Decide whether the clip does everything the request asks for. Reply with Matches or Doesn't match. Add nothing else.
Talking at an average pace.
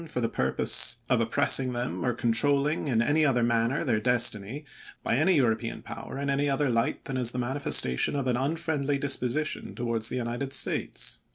Matches